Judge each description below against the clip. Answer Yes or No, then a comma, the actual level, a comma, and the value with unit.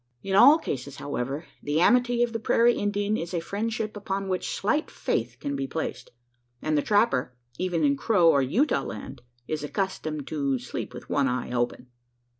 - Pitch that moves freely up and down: Yes, wide, 7.1 semitones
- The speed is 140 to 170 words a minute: No, average, 180 wpm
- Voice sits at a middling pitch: Yes, medium, 165 Hz